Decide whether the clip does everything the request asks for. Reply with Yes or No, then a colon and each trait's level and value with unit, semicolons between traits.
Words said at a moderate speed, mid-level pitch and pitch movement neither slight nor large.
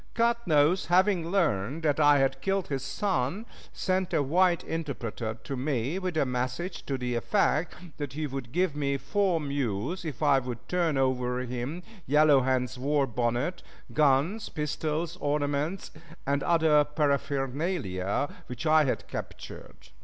Yes: average, 150 wpm; medium, 145 Hz; average, 4.6 semitones